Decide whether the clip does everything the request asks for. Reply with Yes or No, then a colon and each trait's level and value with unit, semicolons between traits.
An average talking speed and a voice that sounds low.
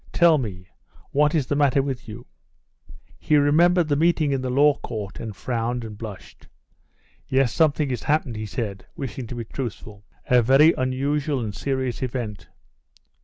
Yes: average, 165 wpm; low, 130 Hz